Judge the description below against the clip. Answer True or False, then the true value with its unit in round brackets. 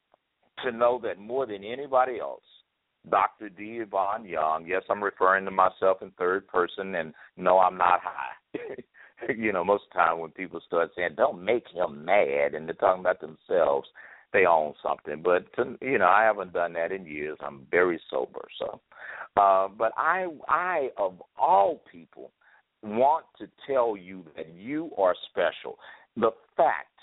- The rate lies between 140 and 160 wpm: False (170 wpm)